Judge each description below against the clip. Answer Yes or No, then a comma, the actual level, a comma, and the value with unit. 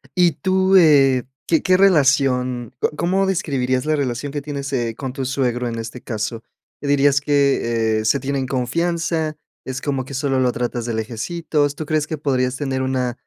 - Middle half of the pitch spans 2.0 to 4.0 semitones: Yes, average, 3.2 semitones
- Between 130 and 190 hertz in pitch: Yes, low, 135 Hz